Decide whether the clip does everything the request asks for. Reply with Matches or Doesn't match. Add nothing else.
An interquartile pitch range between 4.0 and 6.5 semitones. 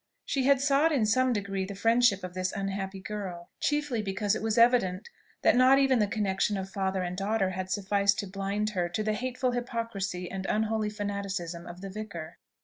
Doesn't match